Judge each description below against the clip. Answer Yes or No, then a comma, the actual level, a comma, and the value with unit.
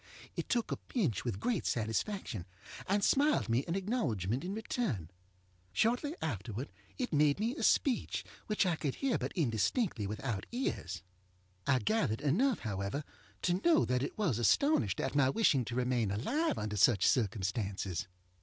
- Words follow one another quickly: No, average, 155 wpm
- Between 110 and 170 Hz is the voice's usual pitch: Yes, low, 135 Hz